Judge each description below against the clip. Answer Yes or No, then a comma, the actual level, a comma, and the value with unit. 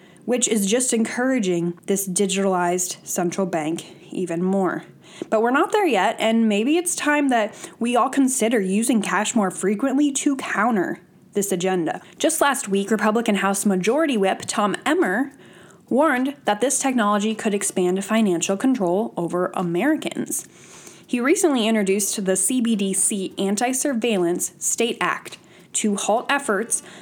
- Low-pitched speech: No, high, 215 Hz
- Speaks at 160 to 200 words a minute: No, average, 140 wpm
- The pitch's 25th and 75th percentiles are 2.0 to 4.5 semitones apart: No, average, 5.2 semitones